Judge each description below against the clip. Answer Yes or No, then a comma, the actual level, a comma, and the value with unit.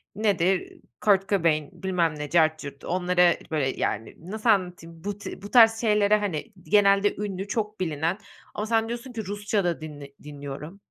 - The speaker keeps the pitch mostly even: No, average, 4.5 semitones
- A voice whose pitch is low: No, high, 190 Hz